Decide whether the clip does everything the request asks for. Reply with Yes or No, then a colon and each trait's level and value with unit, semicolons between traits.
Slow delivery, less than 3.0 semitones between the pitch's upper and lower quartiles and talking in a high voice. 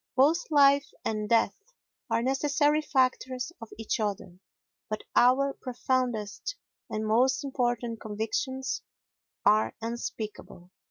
No: slow, 105 wpm; average, 3.7 semitones; high, 245 Hz